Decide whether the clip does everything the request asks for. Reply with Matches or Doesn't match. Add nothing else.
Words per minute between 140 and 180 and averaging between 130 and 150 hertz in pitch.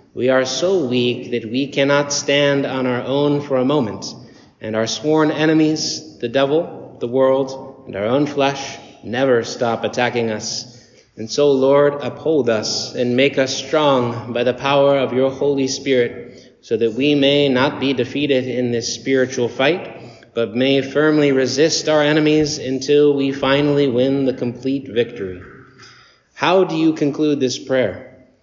Matches